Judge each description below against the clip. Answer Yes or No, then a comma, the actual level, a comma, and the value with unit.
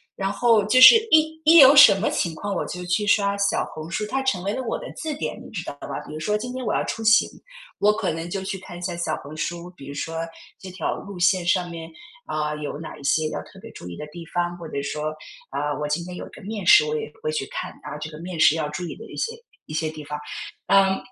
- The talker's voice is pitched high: No, medium, 180 Hz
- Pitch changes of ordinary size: No, wide, 5.7 semitones